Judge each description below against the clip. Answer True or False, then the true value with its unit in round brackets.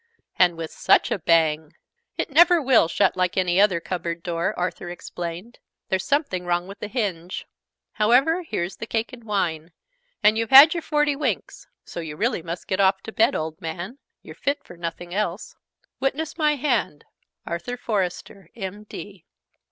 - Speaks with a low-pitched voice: False (190 Hz)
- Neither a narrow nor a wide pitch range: False (6.1 semitones)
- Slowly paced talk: False (165 wpm)